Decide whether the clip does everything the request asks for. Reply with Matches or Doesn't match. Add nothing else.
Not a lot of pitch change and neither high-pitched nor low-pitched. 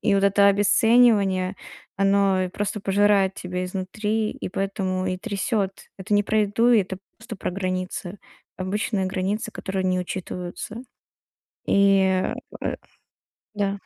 Doesn't match